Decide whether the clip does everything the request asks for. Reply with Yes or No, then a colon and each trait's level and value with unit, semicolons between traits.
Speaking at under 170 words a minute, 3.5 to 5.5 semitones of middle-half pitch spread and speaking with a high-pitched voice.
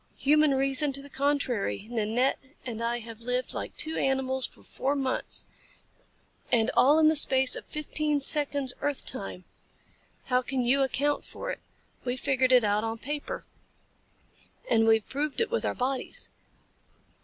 No: average, 155 wpm; average, 3.0 semitones; very high, 265 Hz